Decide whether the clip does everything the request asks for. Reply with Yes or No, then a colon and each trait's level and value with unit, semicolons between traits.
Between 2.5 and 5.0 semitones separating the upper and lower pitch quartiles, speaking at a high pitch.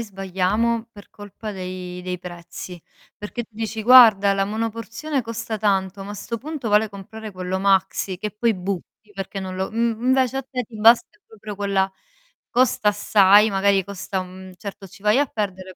Yes: average, 2.8 semitones; high, 205 Hz